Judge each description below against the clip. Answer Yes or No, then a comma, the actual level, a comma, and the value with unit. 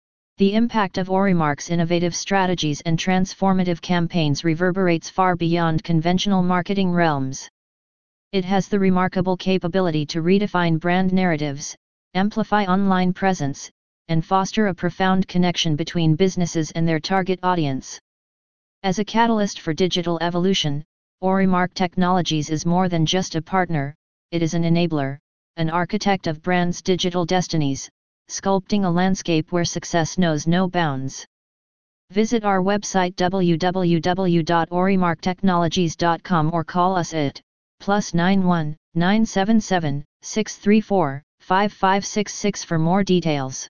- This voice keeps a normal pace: No, slow, 115 wpm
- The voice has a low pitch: No, medium, 180 Hz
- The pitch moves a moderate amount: No, narrow, 2.3 semitones